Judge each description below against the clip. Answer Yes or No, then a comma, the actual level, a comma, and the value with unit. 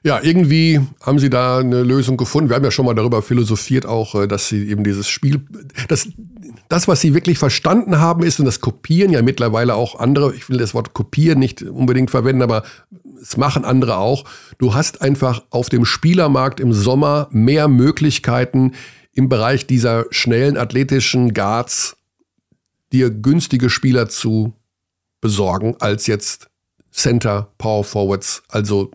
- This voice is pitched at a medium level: No, low, 125 Hz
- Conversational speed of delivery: Yes, average, 160 wpm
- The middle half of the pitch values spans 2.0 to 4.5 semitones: Yes, average, 3.8 semitones